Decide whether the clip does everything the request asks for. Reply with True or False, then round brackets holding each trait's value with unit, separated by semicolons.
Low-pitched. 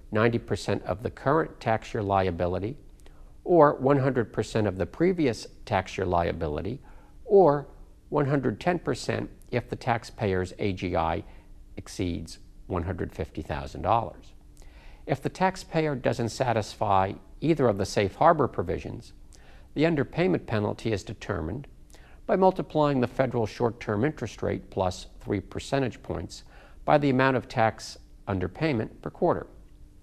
True (110 Hz)